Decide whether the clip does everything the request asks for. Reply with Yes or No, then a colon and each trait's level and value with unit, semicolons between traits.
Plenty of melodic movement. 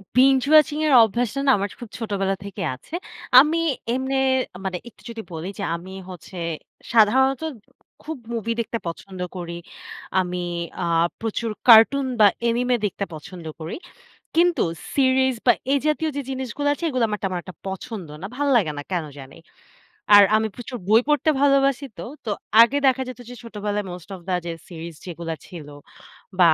Yes: wide, 6.1 semitones